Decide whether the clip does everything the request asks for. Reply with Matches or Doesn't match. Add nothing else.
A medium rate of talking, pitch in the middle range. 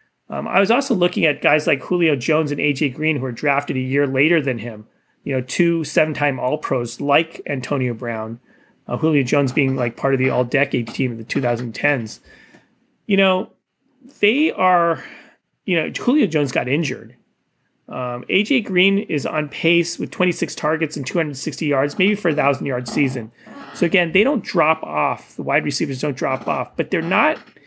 Matches